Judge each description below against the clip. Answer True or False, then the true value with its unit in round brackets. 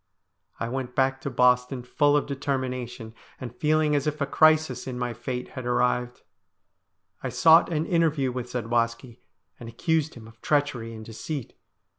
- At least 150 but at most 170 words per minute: True (160 wpm)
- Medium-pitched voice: False (130 Hz)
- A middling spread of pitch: True (3.0 semitones)